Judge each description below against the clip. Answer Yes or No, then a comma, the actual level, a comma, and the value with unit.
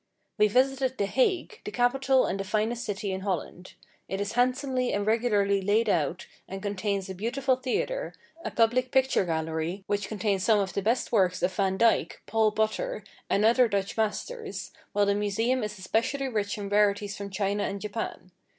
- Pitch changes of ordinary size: Yes, average, 3.8 semitones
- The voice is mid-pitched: No, high, 210 Hz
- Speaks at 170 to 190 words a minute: Yes, average, 180 wpm